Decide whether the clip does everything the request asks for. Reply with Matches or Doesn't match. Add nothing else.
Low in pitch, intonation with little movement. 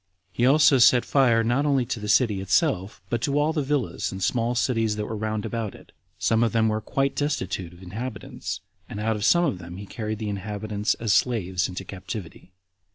Doesn't match